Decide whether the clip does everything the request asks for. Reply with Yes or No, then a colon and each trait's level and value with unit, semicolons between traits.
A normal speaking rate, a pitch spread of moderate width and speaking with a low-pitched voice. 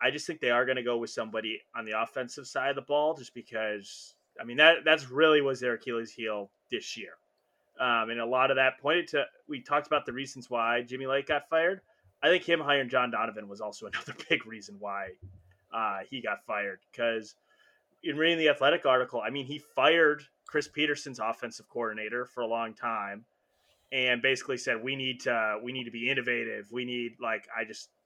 No: fast, 210 wpm; average, 4.1 semitones; low, 125 Hz